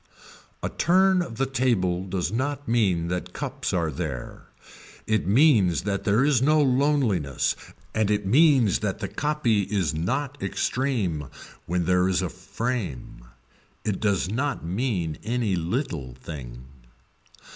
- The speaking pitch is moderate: No, low, 100 Hz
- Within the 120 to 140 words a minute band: Yes, slow, 135 wpm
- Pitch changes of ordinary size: No, wide, 6.7 semitones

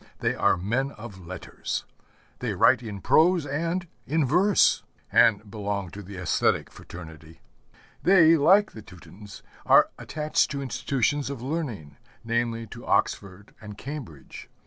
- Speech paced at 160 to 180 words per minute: No, slow, 135 wpm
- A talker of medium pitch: No, low, 115 Hz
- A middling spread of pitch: No, wide, 7.4 semitones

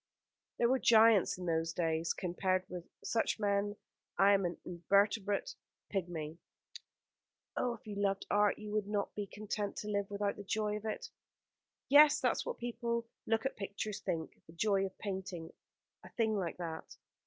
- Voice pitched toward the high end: Yes, high, 200 Hz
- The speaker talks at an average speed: Yes, average, 170 wpm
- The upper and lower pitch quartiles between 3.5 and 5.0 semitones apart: No, average, 3.0 semitones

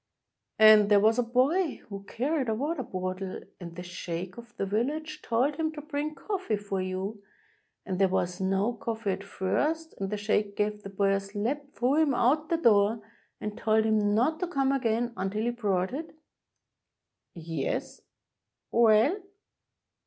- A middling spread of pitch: No, wide, 5.8 semitones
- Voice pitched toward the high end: Yes, high, 220 Hz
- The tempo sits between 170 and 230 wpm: Yes, average, 175 wpm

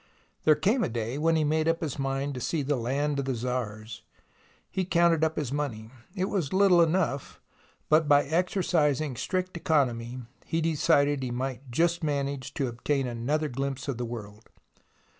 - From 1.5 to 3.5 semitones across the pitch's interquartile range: No, average, 4.2 semitones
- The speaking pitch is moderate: Yes, medium, 145 Hz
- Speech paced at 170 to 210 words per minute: Yes, average, 175 wpm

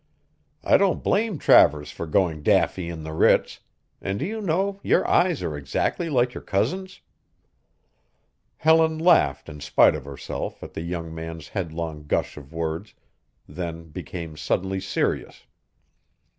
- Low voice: Yes, very low, 85 Hz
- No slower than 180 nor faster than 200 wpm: No, average, 145 wpm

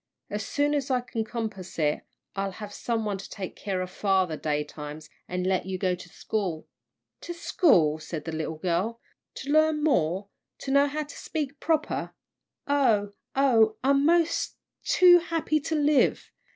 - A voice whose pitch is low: No, high, 220 Hz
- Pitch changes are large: Yes, wide, 8.0 semitones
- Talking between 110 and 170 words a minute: Yes, average, 165 wpm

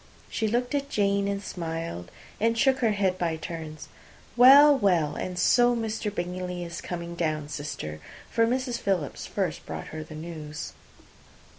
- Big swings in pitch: Yes, wide, 6.0 semitones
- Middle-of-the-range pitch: Yes, medium, 180 Hz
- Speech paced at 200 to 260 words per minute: No, average, 155 wpm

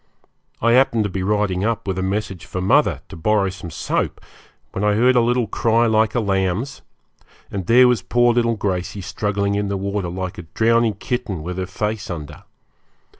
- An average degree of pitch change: Yes, average, 3.6 semitones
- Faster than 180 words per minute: Yes, average, 190 wpm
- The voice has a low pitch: Yes, low, 105 Hz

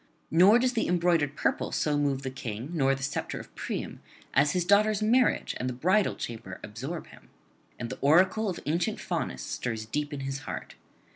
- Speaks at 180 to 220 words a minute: Yes, average, 190 wpm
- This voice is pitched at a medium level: Yes, medium, 150 Hz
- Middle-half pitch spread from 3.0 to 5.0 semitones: No, wide, 5.5 semitones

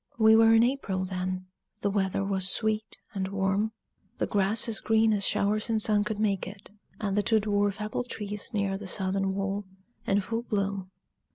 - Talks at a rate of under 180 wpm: No, average, 185 wpm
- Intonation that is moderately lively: No, narrow, 2.0 semitones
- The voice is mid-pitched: No, high, 205 Hz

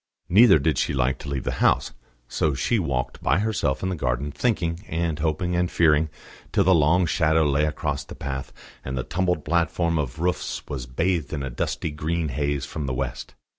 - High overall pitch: No, very low, 80 Hz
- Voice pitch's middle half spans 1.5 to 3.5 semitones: No, average, 3.9 semitones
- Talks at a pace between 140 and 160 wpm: No, average, 200 wpm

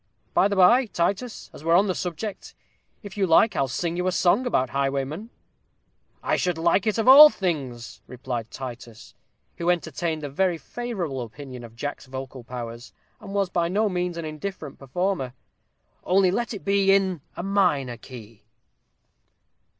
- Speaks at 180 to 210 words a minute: No, average, 165 wpm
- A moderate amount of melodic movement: No, wide, 6.6 semitones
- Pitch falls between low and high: Yes, medium, 170 Hz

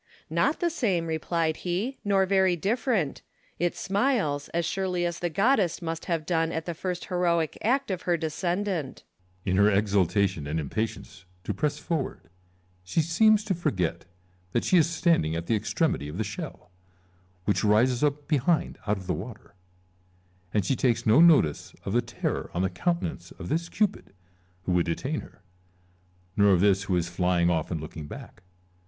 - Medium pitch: Yes, medium, 155 Hz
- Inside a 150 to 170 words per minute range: No, average, 180 wpm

